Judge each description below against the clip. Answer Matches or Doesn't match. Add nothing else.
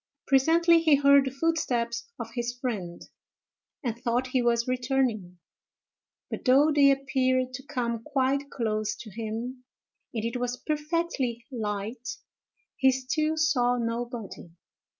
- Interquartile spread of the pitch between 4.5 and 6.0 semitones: Doesn't match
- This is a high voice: Matches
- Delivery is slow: Matches